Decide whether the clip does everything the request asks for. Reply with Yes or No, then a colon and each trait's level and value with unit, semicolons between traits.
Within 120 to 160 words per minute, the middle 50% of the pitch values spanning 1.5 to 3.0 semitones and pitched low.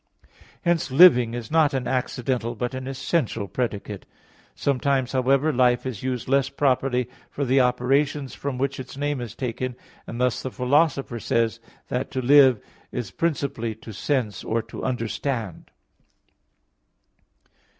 Yes: average, 150 wpm; narrow, 2.5 semitones; low, 130 Hz